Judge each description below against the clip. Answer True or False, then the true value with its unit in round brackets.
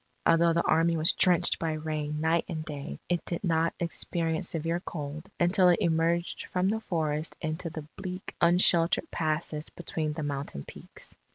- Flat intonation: True (1.7 semitones)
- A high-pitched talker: False (165 Hz)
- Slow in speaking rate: False (165 wpm)